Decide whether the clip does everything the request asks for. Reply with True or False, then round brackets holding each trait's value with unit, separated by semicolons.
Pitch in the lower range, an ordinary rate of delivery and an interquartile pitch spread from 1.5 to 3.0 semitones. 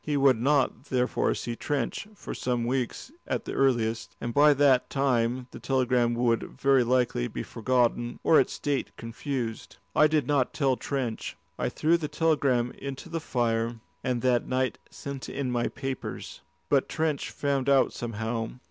True (130 Hz; 165 wpm; 2.7 semitones)